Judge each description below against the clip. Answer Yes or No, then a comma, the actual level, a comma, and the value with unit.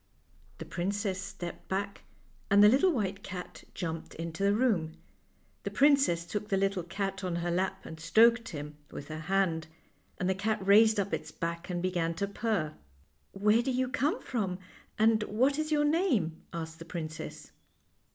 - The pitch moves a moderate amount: Yes, average, 4.5 semitones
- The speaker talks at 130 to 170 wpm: No, average, 180 wpm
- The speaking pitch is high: Yes, high, 195 Hz